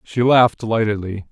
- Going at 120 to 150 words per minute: Yes, slow, 135 wpm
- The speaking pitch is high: No, low, 110 Hz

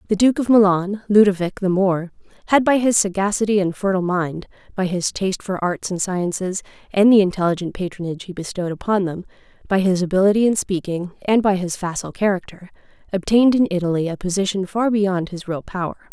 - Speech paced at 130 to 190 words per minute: Yes, average, 180 wpm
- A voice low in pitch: No, high, 190 Hz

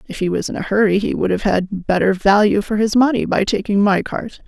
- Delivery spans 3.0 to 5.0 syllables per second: No, 5.6 syllables/s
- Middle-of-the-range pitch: No, high, 205 Hz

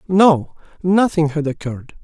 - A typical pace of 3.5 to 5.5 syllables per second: Yes, 4.5 syllables/s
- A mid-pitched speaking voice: Yes, medium, 165 Hz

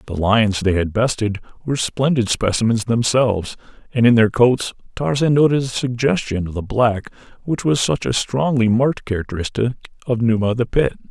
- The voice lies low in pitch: Yes, low, 115 Hz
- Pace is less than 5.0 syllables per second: No, 5.4 syllables/s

